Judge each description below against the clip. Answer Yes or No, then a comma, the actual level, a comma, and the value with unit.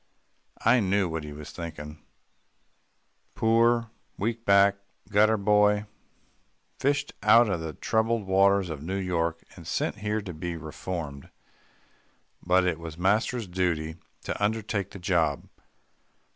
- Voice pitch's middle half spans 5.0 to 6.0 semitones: No, average, 4.2 semitones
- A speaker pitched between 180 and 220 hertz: No, very low, 95 Hz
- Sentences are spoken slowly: Yes, slow, 130 wpm